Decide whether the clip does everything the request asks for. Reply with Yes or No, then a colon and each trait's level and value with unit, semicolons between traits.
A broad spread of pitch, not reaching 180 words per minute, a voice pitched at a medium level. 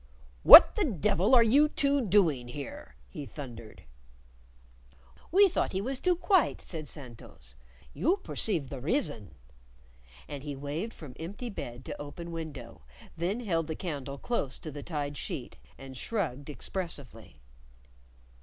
Yes: wide, 7.8 semitones; average, 140 wpm; medium, 155 Hz